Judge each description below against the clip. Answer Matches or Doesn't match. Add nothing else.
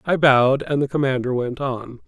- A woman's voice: Doesn't match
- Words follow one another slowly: Doesn't match